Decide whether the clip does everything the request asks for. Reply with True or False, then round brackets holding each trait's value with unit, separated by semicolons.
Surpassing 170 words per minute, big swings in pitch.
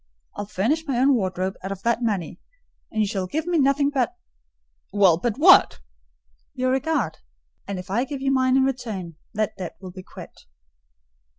True (180 wpm; 6.0 semitones)